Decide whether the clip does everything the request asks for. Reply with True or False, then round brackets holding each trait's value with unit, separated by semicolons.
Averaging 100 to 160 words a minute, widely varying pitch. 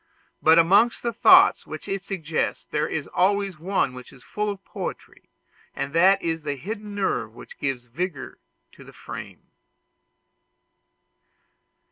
True (140 wpm; 5.7 semitones)